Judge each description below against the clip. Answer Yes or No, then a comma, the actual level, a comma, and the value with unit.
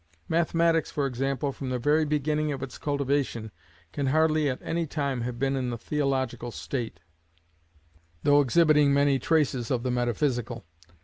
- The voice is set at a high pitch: No, medium, 140 Hz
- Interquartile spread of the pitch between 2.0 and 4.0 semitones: Yes, average, 3.1 semitones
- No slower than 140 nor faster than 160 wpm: Yes, average, 150 wpm